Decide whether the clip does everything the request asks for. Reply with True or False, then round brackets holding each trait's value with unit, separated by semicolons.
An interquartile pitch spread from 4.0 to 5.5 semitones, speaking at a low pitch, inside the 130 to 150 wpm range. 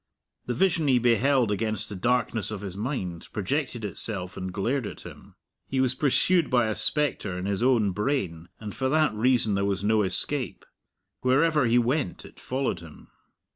False (4.8 semitones; 115 Hz; 175 wpm)